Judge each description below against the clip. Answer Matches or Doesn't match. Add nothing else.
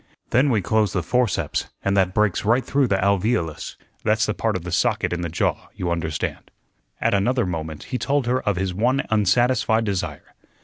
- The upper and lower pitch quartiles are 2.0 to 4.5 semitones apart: Doesn't match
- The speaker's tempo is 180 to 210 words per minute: Matches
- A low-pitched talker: Matches